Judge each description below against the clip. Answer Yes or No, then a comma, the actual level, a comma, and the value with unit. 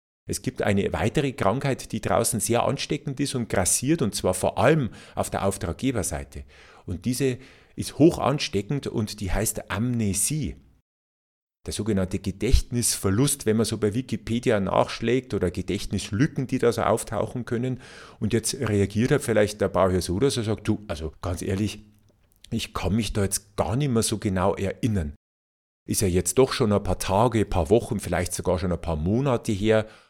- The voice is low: Yes, low, 105 Hz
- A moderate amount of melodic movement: Yes, average, 4.2 semitones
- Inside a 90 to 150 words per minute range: No, average, 175 wpm